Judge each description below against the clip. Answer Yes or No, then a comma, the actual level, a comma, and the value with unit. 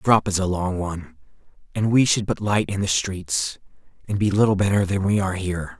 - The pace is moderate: No, fast, 230 wpm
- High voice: No, very low, 95 Hz